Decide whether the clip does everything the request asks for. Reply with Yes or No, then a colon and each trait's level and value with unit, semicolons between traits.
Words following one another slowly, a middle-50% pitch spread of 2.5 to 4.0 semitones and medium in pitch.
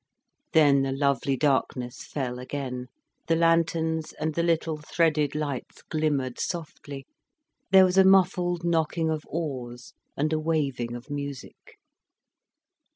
Yes: slow, 125 wpm; average, 3.4 semitones; medium, 150 Hz